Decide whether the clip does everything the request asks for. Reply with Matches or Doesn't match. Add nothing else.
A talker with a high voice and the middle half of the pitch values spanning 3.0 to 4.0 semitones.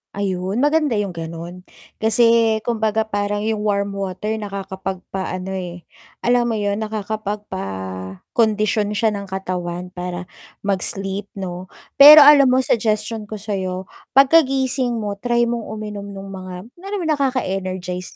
Matches